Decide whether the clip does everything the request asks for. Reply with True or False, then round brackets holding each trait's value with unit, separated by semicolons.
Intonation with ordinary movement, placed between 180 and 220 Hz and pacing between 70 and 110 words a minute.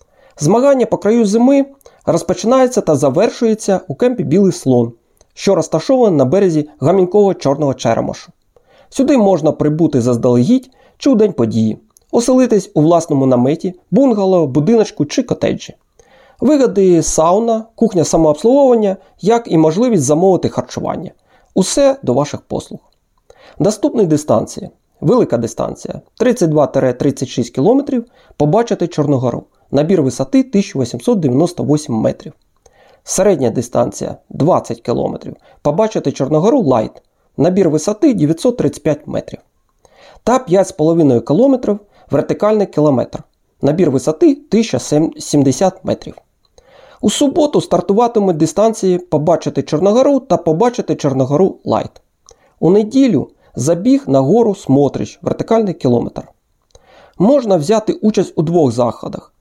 False (7.2 semitones; 185 Hz; 105 wpm)